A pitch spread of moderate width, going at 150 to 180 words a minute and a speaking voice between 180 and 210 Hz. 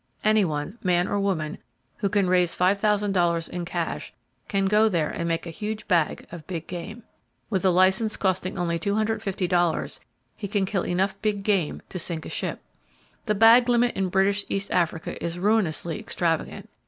Yes: average, 3.1 semitones; average, 165 wpm; high, 190 Hz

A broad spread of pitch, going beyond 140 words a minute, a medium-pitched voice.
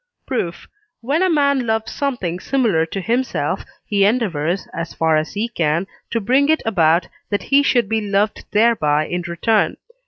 No: wide, 6.6 semitones; average, 175 wpm; high, 210 Hz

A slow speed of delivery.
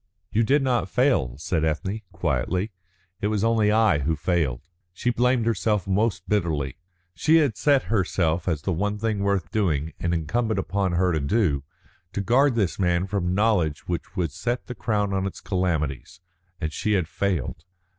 No: average, 175 wpm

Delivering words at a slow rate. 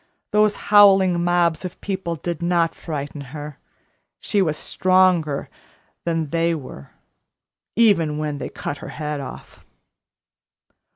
Yes: slow, 120 wpm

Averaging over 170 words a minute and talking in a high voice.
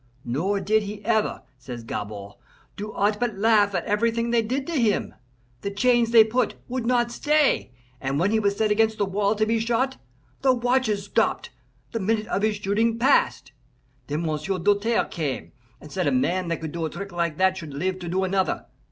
Yes: average, 200 wpm; high, 205 Hz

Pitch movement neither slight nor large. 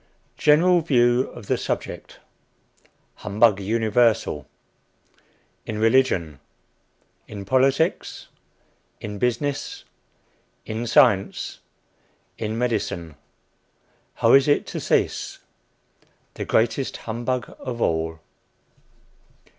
Yes: average, 4.0 semitones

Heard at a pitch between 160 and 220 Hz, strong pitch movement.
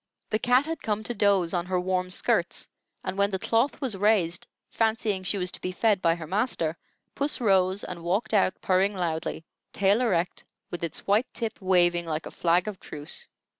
No: high, 190 Hz; average, 3.6 semitones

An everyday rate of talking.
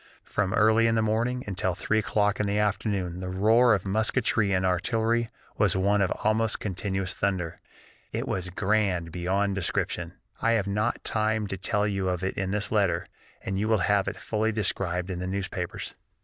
Yes: average, 180 wpm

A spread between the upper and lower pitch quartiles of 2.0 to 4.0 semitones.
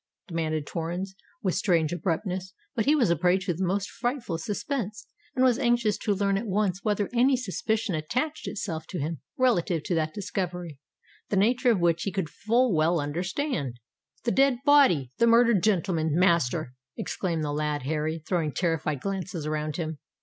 No: wide, 5.5 semitones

